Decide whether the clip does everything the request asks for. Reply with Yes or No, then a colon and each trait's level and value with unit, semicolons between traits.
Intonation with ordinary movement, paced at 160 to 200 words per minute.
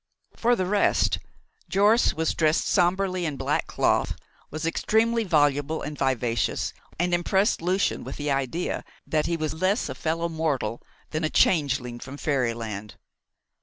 No: average, 4.9 semitones; average, 145 wpm